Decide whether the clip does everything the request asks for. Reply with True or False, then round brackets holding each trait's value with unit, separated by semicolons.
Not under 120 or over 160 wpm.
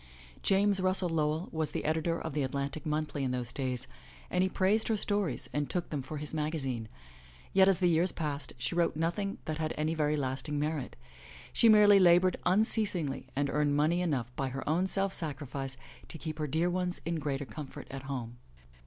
False (195 wpm)